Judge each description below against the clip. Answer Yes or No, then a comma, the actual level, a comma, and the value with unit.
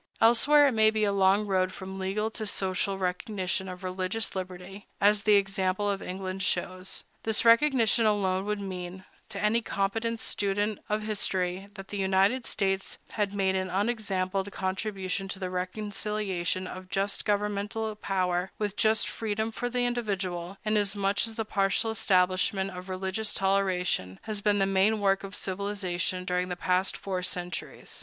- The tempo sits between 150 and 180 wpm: Yes, average, 160 wpm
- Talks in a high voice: Yes, high, 195 Hz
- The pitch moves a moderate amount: No, narrow, 2.2 semitones